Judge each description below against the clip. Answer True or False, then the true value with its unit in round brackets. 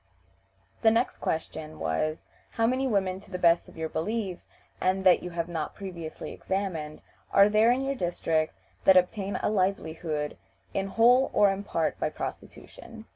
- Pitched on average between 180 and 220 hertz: True (190 Hz)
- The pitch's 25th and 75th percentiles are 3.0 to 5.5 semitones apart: True (4.5 semitones)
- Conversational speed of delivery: True (165 wpm)